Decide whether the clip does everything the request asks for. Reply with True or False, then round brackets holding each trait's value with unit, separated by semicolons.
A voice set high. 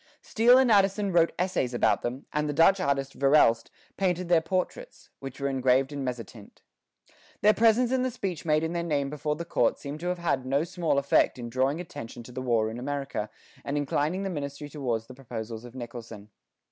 False (145 Hz)